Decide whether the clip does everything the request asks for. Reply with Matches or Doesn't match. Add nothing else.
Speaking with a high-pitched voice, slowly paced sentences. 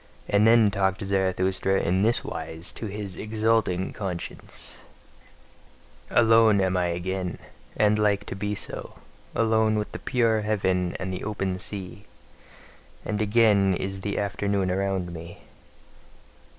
Doesn't match